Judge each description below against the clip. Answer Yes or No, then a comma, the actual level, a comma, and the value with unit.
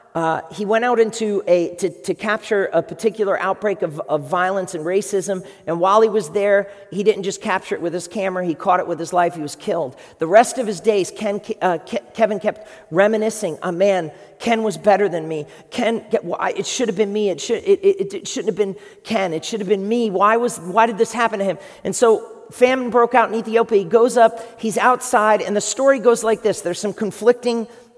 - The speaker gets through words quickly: Yes, fast, 240 wpm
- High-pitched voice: Yes, high, 210 Hz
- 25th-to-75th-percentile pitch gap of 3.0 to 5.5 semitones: Yes, average, 3.4 semitones